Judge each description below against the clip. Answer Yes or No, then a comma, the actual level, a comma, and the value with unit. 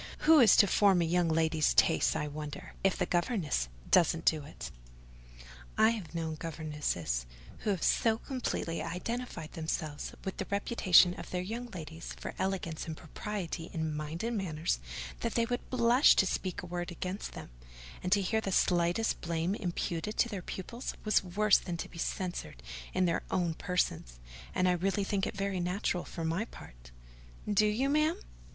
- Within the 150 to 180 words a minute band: Yes, average, 175 wpm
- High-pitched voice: No, medium, 180 Hz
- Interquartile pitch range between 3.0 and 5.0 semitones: Yes, average, 4.2 semitones